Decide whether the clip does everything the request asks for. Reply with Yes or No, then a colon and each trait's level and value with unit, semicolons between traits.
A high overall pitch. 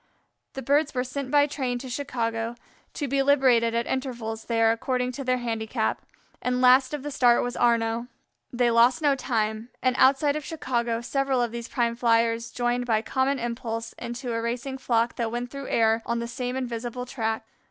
Yes: high, 245 Hz